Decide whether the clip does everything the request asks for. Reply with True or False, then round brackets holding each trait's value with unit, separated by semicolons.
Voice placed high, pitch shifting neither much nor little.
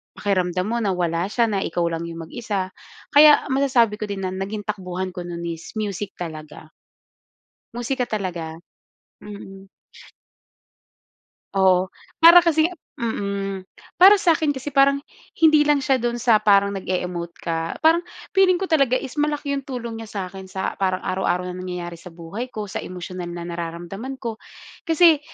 False (200 Hz; 6.7 semitones)